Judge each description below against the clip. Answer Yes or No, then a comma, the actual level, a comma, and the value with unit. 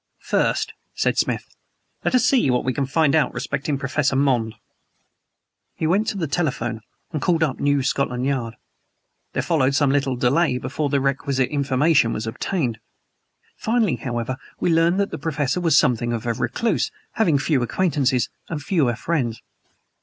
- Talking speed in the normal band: Yes, average, 160 wpm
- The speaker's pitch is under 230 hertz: Yes, medium, 140 Hz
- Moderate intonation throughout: Yes, average, 4.3 semitones